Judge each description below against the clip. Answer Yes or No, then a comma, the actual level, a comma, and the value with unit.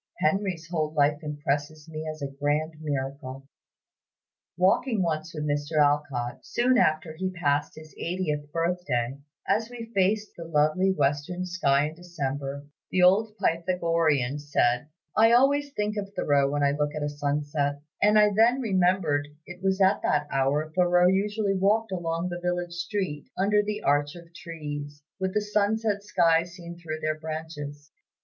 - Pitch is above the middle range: No, medium, 165 Hz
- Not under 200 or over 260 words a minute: No, average, 160 wpm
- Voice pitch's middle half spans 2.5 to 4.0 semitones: No, average, 4.5 semitones